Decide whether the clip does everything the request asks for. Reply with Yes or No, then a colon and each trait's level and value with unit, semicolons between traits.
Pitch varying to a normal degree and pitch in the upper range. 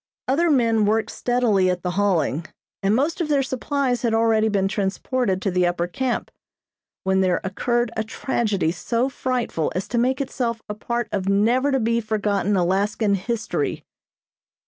Yes: average, 4.2 semitones; high, 220 Hz